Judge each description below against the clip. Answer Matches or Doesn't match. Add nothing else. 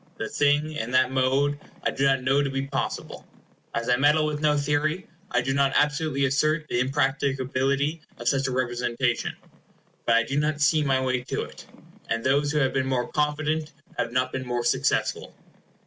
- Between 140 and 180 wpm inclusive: Doesn't match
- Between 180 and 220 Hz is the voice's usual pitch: Doesn't match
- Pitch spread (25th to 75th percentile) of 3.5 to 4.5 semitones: Doesn't match